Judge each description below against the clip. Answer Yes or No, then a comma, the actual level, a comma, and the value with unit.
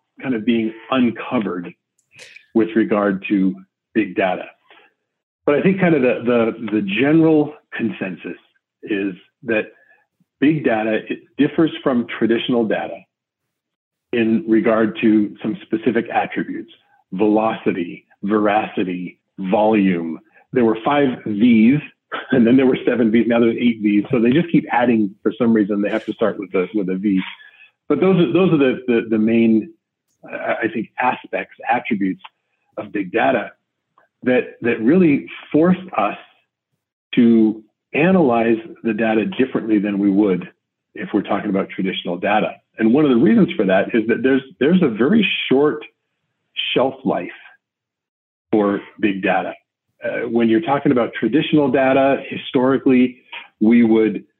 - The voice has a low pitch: Yes, low, 115 Hz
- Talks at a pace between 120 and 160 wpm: Yes, average, 145 wpm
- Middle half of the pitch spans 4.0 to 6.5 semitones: Yes, average, 4.4 semitones